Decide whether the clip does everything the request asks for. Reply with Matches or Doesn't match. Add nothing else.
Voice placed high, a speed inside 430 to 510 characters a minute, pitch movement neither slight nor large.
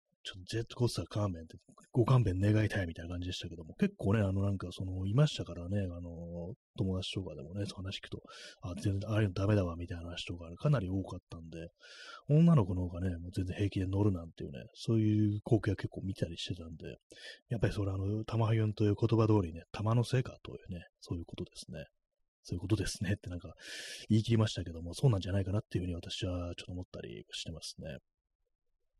Doesn't match